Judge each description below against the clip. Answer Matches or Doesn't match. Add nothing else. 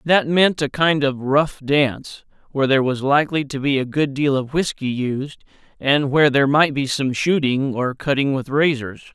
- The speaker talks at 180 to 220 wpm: Matches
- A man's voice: Matches